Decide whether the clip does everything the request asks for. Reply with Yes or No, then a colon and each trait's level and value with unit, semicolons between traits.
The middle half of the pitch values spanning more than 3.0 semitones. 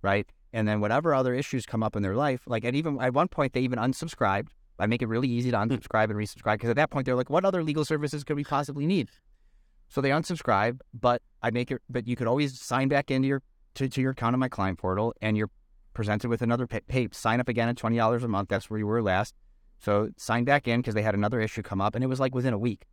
Yes: average, 3.6 semitones